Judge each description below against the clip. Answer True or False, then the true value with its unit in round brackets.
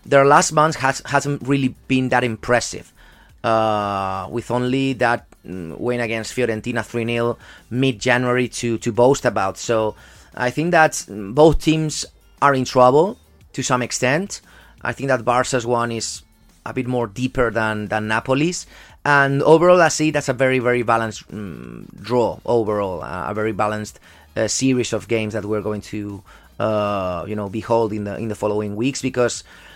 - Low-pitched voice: True (120 Hz)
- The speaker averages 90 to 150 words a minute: False (170 wpm)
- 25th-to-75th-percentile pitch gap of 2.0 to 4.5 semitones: True (3.6 semitones)